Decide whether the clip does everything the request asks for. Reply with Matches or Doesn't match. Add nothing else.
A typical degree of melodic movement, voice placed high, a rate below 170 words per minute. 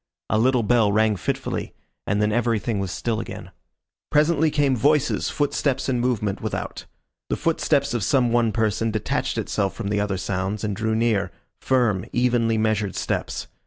Doesn't match